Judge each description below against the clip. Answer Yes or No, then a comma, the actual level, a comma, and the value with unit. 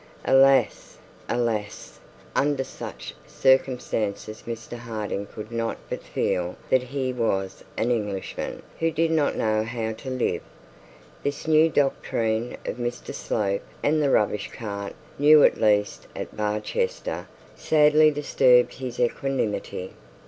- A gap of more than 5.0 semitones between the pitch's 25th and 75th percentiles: No, average, 4.5 semitones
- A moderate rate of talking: No, slow, 125 wpm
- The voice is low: Yes, low, 120 Hz